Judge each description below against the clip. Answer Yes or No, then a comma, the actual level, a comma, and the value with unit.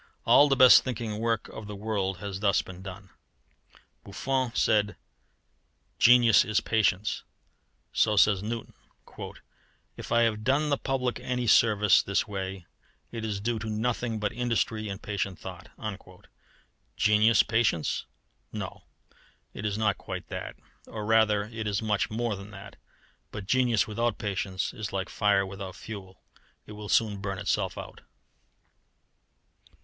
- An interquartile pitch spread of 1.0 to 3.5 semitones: Yes, narrow, 2.5 semitones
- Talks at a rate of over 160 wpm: No, average, 145 wpm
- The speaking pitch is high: No, low, 105 Hz